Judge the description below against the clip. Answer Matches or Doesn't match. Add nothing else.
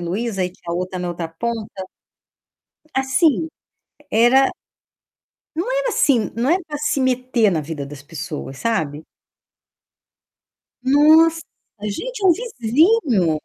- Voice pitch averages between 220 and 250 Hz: Matches